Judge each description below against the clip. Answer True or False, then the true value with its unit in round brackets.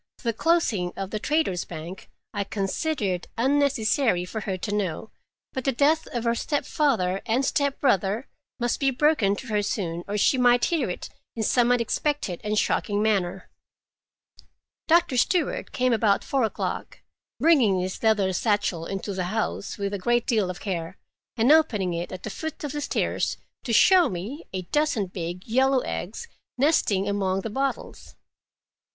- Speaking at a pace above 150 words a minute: True (160 wpm)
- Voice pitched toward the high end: True (220 Hz)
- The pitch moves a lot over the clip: True (5.9 semitones)